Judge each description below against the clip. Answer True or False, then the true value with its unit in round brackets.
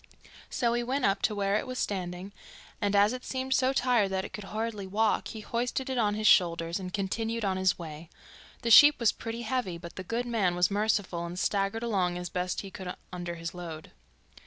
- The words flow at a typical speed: False (215 wpm)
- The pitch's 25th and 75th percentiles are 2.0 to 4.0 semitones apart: False (4.4 semitones)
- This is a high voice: True (200 Hz)